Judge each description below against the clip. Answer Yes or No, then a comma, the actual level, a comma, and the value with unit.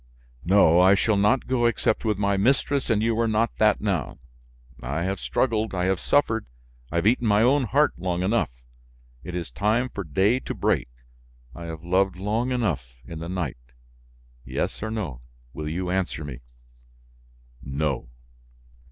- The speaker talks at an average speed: Yes, average, 165 wpm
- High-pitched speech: No, low, 100 Hz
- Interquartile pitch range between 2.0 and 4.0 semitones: No, average, 4.8 semitones